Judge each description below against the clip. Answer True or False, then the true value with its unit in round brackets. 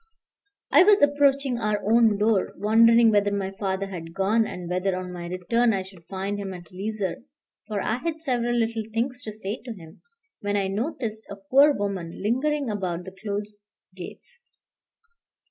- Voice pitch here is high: True (210 Hz)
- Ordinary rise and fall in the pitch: True (3.6 semitones)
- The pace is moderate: True (170 wpm)